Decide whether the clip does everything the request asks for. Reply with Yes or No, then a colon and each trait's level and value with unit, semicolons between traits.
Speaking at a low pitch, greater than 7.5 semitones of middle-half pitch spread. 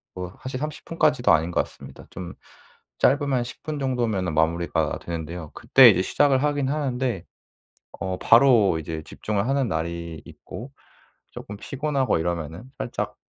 Yes: low, 110 Hz; wide, 7.9 semitones